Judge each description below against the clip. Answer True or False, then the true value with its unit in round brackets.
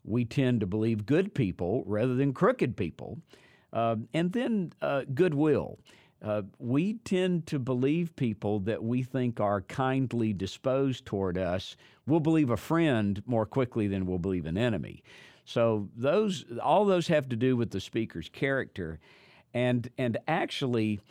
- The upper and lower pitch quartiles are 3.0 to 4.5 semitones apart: False (5.4 semitones)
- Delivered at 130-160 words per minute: True (155 wpm)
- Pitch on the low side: True (125 Hz)